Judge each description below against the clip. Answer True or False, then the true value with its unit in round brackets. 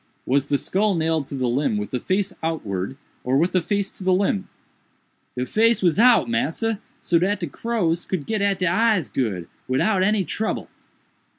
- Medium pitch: True (175 Hz)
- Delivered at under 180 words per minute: False (190 wpm)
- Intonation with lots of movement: True (6.8 semitones)